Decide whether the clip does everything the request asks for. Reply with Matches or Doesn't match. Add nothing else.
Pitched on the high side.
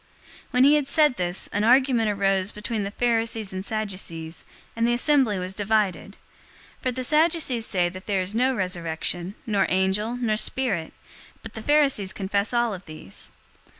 Matches